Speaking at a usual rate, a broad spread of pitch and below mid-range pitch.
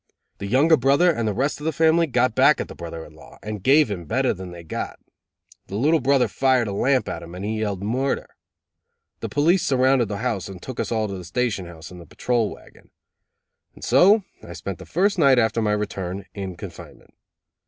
No: fast, 215 wpm; wide, 5.9 semitones; low, 115 Hz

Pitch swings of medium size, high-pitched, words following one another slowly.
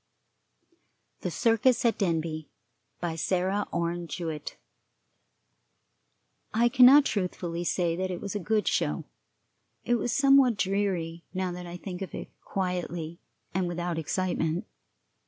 No: average, 3.3 semitones; medium, 180 Hz; slow, 125 wpm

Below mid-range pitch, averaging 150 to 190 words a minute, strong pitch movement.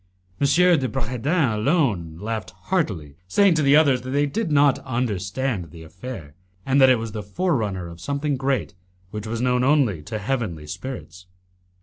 Yes: low, 125 Hz; average, 170 wpm; wide, 6.3 semitones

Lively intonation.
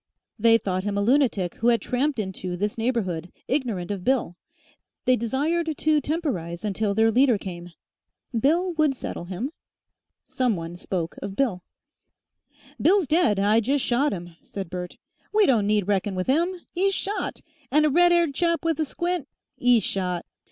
Yes: wide, 7.8 semitones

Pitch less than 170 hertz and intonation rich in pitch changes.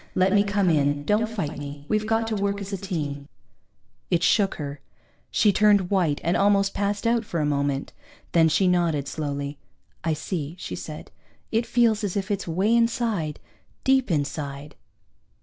No: medium, 185 Hz; wide, 5.8 semitones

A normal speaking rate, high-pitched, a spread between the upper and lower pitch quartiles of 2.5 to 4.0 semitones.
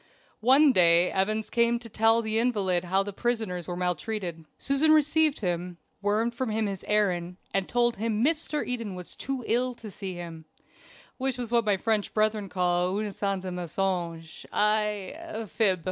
No: average, 170 wpm; high, 210 Hz; average, 4.4 semitones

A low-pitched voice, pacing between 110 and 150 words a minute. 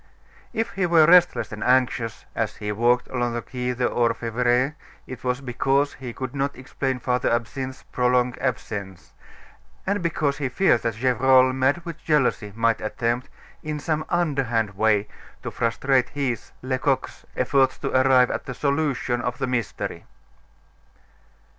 Yes: low, 130 Hz; average, 145 wpm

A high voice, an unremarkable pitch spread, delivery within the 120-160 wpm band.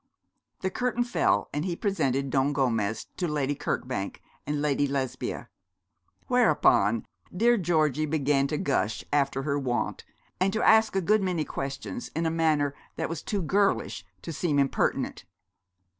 No: medium, 150 Hz; average, 4.6 semitones; average, 150 wpm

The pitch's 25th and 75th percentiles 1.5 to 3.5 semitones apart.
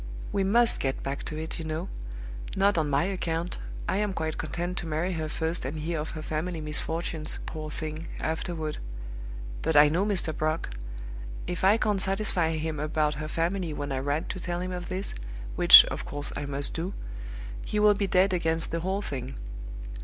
Yes: average, 3.2 semitones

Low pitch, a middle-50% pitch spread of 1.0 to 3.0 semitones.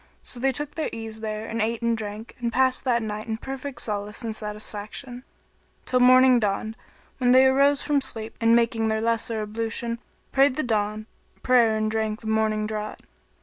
No: high, 225 Hz; narrow, 2.6 semitones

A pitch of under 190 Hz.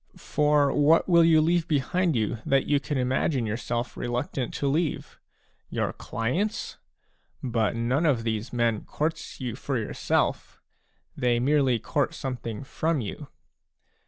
Yes: low, 135 Hz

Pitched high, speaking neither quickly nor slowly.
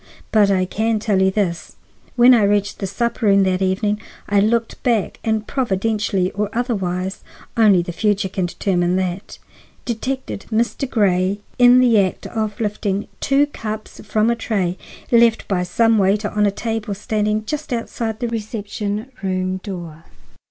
Yes: high, 210 Hz; average, 155 wpm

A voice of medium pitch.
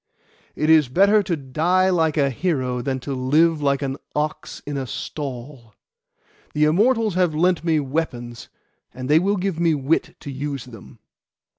Yes: medium, 150 Hz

